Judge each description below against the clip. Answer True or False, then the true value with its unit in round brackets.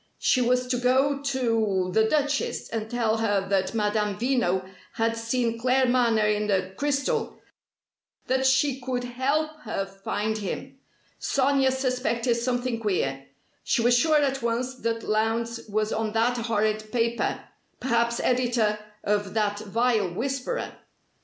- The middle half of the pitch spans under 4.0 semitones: True (3.1 semitones)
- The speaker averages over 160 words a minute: False (135 wpm)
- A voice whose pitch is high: True (235 Hz)